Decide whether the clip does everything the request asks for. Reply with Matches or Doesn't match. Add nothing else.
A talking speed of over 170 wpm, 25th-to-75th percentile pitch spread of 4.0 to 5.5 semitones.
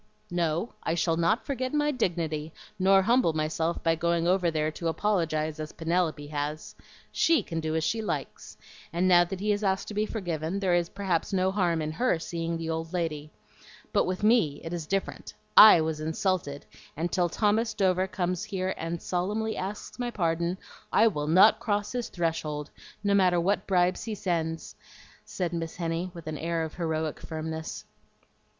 Doesn't match